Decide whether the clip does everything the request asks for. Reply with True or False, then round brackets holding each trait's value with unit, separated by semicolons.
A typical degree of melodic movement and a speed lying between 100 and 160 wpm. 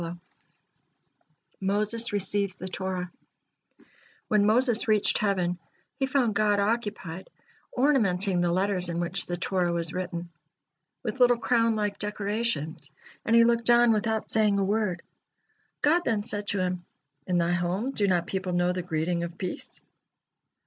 True (3.8 semitones; 145 wpm)